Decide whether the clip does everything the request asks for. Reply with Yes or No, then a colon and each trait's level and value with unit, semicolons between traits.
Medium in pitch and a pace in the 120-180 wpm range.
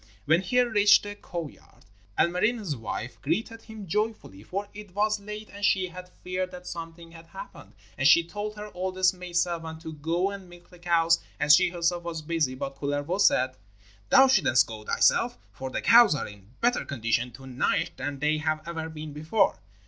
No: medium, 170 Hz; average, 190 wpm